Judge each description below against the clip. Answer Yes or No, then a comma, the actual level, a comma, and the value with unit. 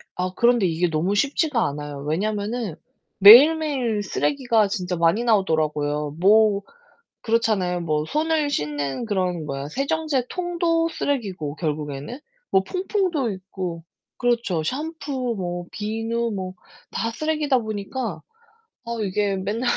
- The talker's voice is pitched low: No, high, 210 Hz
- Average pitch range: No, wide, 6.7 semitones